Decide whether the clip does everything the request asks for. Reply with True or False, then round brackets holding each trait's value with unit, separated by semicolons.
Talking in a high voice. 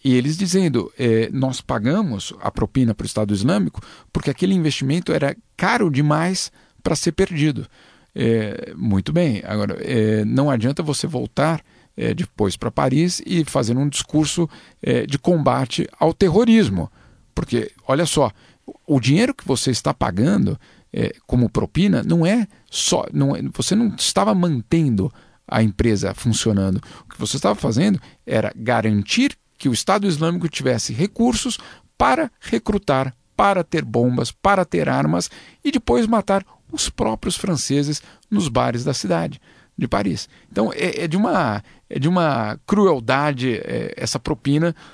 False (145 Hz)